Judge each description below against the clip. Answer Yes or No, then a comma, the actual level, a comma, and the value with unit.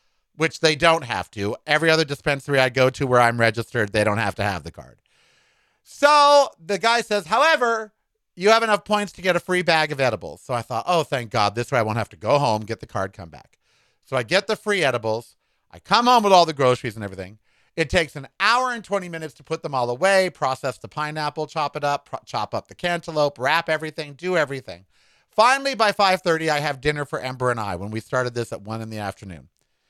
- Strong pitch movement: Yes, wide, 7.6 semitones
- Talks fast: Yes, fast, 235 wpm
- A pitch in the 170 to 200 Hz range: No, medium, 150 Hz